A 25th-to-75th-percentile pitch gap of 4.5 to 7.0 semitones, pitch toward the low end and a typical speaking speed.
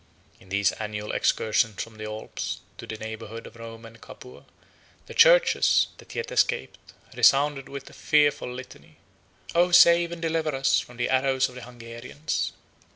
Yes: average, 5.1 semitones; low, 125 Hz; average, 160 wpm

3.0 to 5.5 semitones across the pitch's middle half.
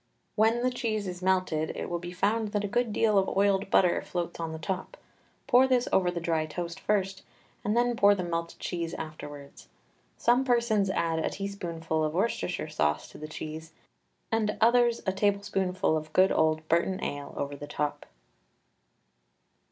Yes: average, 4.6 semitones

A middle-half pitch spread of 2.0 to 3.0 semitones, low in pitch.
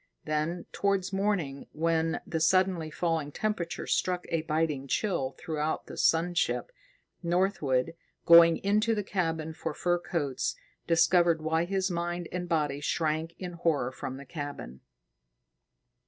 No: narrow, 2.6 semitones; medium, 165 Hz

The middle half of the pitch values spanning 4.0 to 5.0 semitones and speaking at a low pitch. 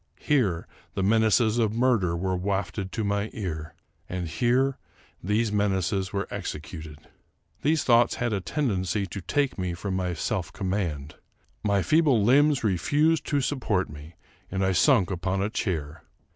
Yes: average, 4.6 semitones; low, 100 Hz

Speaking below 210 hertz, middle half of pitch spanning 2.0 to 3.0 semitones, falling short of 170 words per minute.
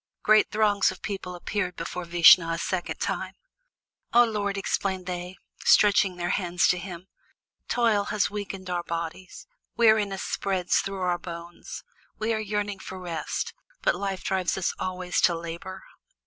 Yes: medium, 185 Hz; narrow, 2.5 semitones; average, 150 wpm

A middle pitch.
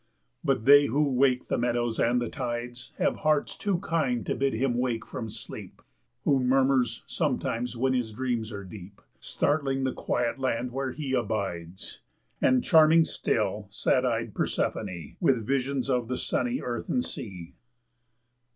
No: low, 125 Hz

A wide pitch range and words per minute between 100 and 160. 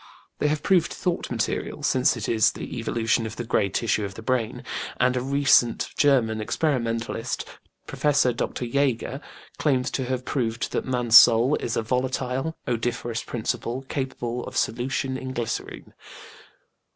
No: narrow, 2.4 semitones; average, 150 wpm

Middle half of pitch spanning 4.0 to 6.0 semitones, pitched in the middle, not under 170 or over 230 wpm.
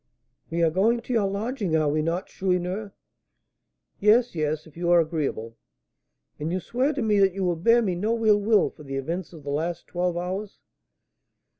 Yes: average, 4.5 semitones; medium, 180 Hz; average, 185 wpm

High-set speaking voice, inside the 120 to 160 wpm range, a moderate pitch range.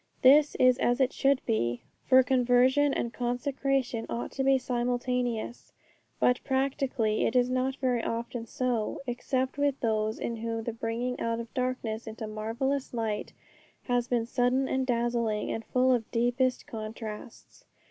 No: high, 245 Hz; average, 150 wpm; narrow, 2.2 semitones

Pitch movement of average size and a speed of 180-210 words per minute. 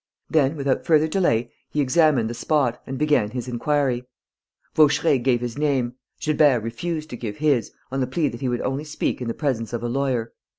Yes: average, 3.9 semitones; average, 200 wpm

